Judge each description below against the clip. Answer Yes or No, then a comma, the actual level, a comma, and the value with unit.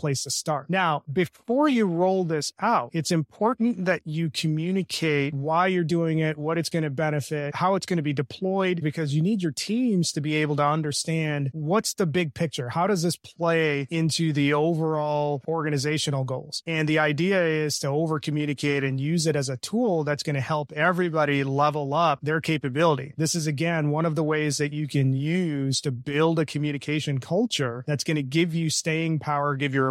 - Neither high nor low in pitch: Yes, medium, 155 Hz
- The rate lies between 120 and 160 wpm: No, average, 200 wpm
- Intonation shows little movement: Yes, narrow, 2.3 semitones